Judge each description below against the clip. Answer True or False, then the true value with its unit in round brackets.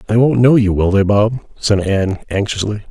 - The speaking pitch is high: False (105 Hz)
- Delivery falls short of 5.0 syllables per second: False (5.2 syllables/s)